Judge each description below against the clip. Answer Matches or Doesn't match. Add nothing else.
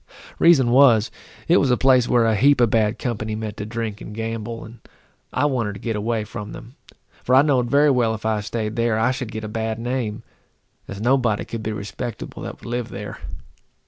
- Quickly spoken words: Matches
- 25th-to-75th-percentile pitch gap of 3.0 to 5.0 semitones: Doesn't match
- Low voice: Matches